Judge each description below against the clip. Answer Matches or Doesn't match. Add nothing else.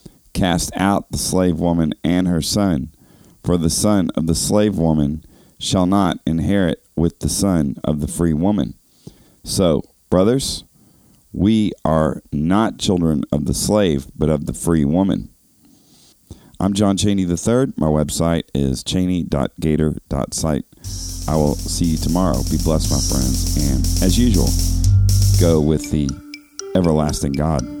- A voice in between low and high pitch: Doesn't match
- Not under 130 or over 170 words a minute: Matches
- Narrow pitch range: Doesn't match